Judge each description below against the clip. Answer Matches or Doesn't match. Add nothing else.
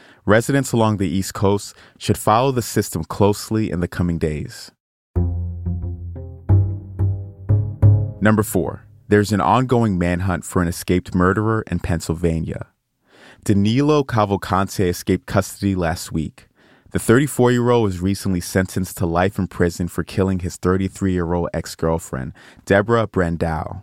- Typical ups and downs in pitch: Matches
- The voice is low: Matches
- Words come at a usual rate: Doesn't match